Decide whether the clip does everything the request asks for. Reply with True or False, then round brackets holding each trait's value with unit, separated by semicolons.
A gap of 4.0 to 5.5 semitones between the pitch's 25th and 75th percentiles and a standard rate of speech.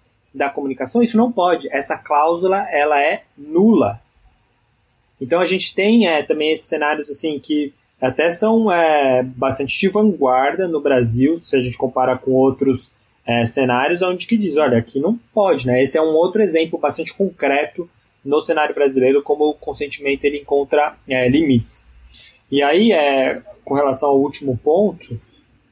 True (4.6 semitones; 160 wpm)